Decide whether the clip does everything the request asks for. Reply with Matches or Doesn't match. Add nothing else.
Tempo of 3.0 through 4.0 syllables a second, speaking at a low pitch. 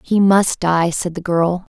Doesn't match